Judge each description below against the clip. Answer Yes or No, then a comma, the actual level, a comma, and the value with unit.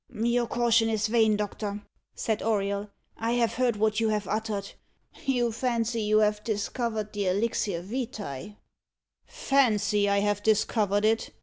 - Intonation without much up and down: Yes, narrow, 2.0 semitones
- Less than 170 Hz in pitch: No, high, 215 Hz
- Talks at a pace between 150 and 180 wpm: No, average, 140 wpm